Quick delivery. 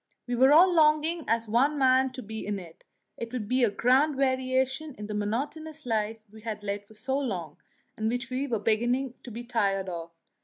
Yes: fast, 220 wpm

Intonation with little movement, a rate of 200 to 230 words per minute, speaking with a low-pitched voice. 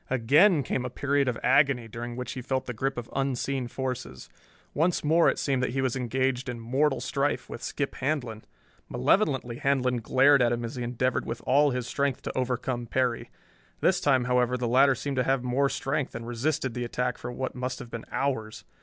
Yes: narrow, 2.1 semitones; fast, 205 wpm; low, 130 Hz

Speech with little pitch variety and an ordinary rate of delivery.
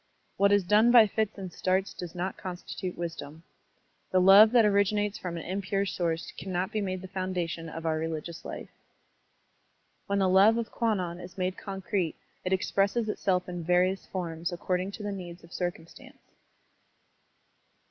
Yes: narrow, 2.3 semitones; average, 160 wpm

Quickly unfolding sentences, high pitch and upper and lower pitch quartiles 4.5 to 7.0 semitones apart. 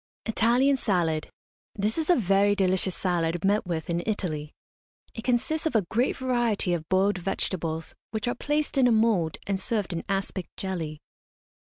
No: average, 165 wpm; high, 195 Hz; average, 5.0 semitones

